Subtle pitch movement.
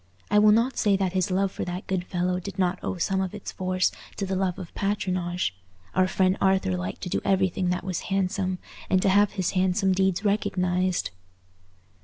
Yes: narrow, 1.2 semitones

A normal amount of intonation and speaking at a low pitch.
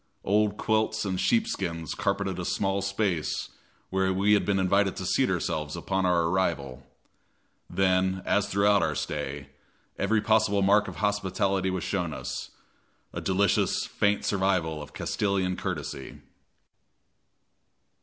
No: narrow, 2.3 semitones; very low, 95 Hz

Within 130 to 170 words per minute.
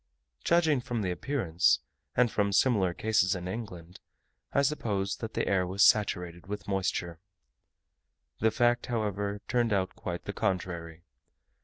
Yes: average, 140 wpm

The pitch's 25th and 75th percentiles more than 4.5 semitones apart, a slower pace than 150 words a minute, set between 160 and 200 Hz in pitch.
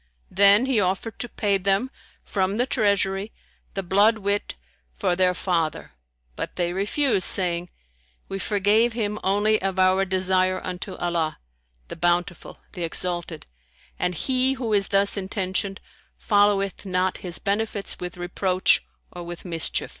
No: narrow, 2.4 semitones; average, 140 wpm; high, 190 Hz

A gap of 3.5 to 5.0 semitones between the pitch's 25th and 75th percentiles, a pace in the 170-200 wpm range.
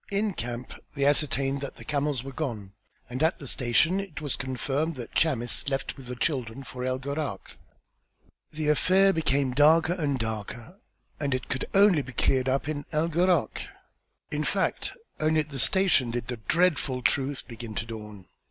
Yes: average, 3.9 semitones; average, 175 wpm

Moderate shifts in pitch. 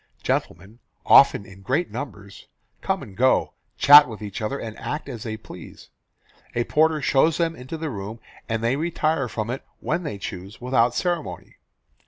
No: wide, 5.8 semitones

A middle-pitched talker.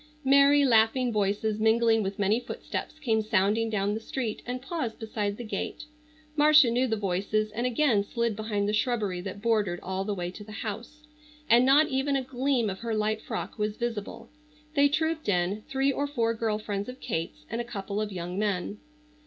No: high, 220 Hz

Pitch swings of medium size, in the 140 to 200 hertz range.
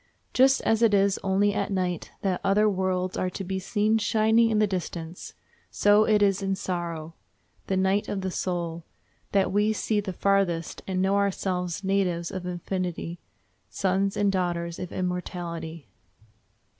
No: narrow, 2.3 semitones; high, 190 Hz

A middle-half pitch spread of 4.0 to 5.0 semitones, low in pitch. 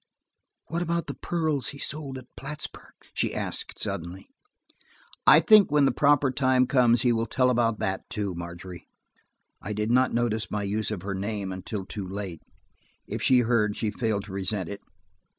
Yes: average, 4.7 semitones; low, 115 Hz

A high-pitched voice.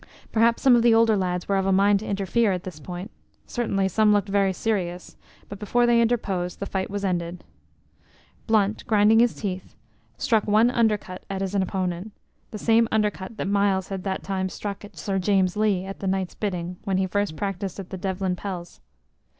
Yes: high, 195 Hz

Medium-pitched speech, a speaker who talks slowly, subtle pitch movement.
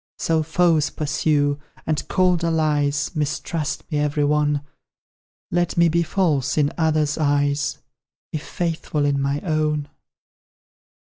Yes: medium, 150 Hz; slow, 120 wpm; narrow, 1.9 semitones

